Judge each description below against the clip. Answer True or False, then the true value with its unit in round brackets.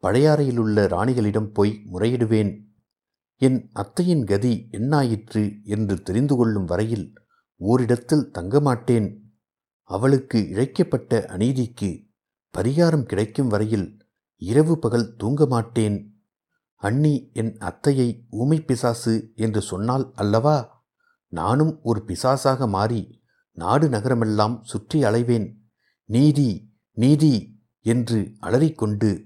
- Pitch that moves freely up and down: False (3.8 semitones)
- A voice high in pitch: False (115 Hz)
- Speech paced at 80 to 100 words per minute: True (90 wpm)